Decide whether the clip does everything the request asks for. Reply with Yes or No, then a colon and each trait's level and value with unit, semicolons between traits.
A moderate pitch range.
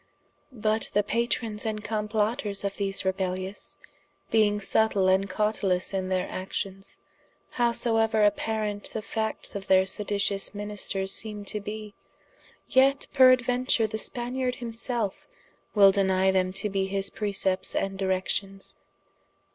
No: narrow, 2.3 semitones